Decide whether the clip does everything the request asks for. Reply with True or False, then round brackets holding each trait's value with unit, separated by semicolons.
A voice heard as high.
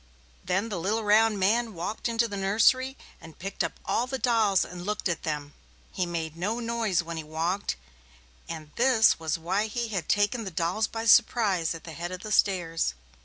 True (195 Hz)